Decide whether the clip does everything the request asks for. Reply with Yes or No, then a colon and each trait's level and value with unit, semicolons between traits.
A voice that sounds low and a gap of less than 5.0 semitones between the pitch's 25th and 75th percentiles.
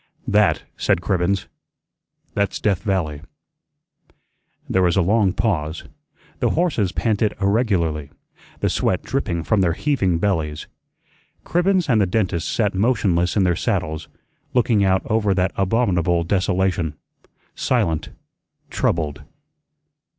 Yes: very low, 95 Hz; average, 4.0 semitones